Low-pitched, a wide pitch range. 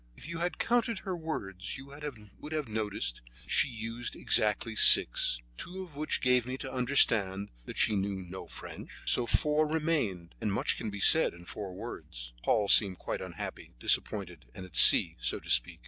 Yes: low, 110 Hz; wide, 7.7 semitones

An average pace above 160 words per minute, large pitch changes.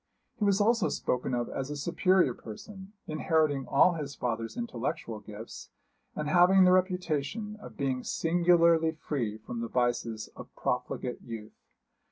No: average, 145 wpm; wide, 6.9 semitones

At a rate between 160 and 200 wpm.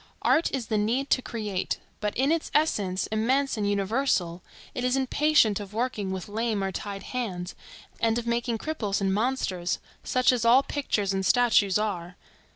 Yes: average, 170 wpm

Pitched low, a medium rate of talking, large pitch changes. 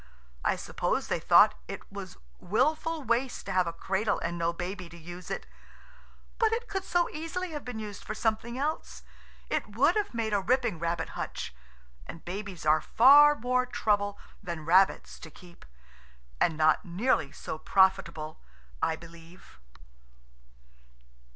No: high, 205 Hz; average, 150 wpm; wide, 6.9 semitones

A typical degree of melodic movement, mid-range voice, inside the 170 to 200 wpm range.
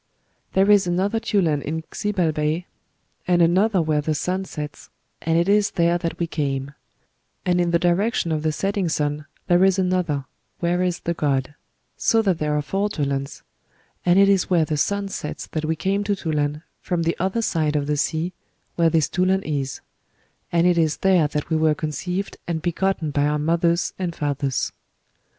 Yes: average, 3.6 semitones; medium, 170 Hz; average, 185 wpm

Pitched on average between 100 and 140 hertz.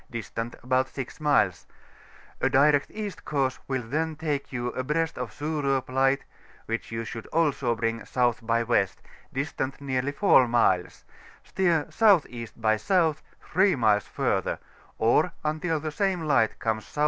Yes: low, 135 Hz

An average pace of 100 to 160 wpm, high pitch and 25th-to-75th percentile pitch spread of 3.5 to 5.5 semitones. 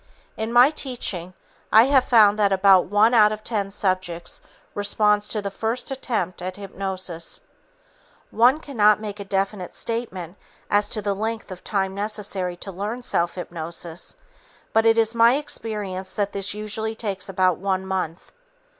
No: average, 155 wpm; high, 205 Hz; average, 2.8 semitones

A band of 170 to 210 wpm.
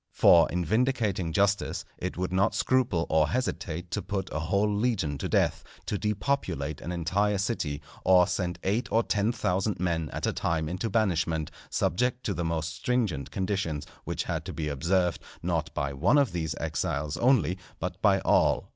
Yes: average, 175 wpm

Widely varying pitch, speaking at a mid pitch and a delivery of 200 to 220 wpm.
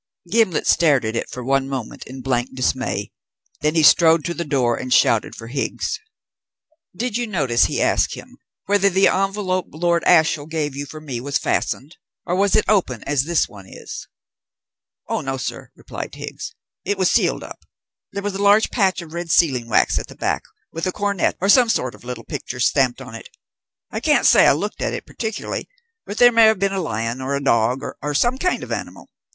Yes: wide, 7.0 semitones; medium, 155 Hz; fast, 205 wpm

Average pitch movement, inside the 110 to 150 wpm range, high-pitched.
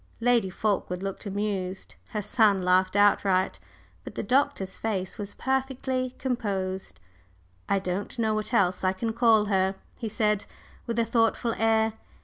Yes: average, 3.2 semitones; average, 145 wpm; high, 210 Hz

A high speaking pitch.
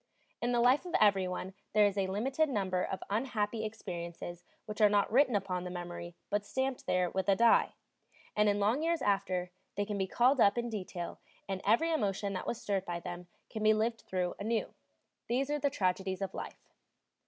Yes: high, 205 Hz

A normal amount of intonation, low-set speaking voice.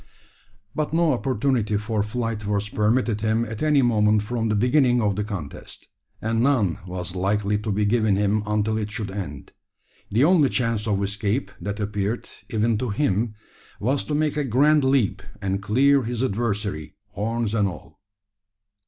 Yes: average, 3.2 semitones; low, 110 Hz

